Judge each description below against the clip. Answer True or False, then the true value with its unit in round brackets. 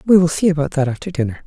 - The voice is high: False (180 Hz)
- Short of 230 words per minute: False (285 wpm)